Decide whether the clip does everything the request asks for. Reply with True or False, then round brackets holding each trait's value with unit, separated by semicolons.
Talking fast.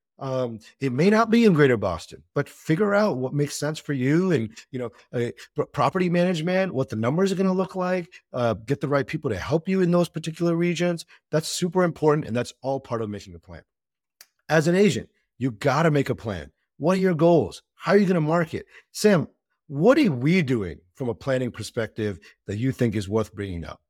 True (220 wpm)